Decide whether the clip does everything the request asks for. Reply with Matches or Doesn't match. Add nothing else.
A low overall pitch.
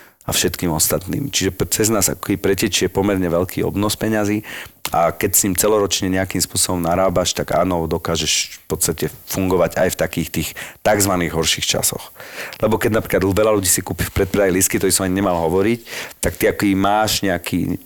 Matches